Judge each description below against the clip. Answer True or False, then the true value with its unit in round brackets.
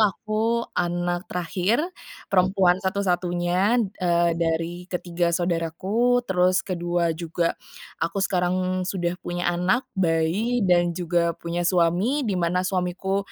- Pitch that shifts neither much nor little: False (1.8 semitones)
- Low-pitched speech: False (180 Hz)